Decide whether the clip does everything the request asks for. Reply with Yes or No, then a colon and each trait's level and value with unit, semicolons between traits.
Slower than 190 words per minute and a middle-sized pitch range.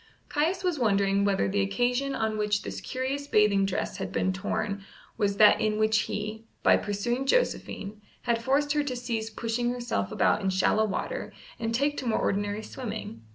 Yes: average, 180 wpm; average, 3.7 semitones